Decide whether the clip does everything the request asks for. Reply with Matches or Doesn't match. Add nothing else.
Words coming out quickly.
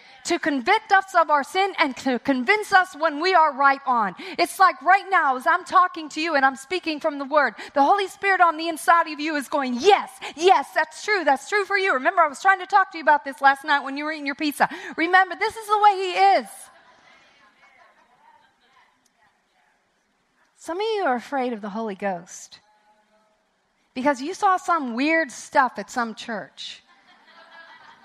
Doesn't match